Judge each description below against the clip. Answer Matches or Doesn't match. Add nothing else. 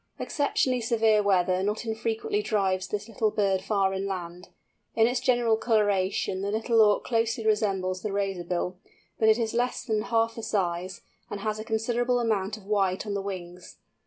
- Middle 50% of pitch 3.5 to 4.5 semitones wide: Doesn't match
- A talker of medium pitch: Doesn't match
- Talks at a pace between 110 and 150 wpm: Doesn't match